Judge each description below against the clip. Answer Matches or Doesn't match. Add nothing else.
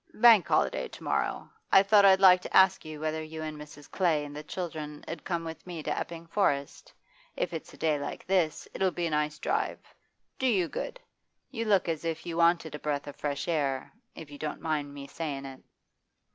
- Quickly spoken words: Matches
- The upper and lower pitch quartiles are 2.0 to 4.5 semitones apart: Matches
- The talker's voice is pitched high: Doesn't match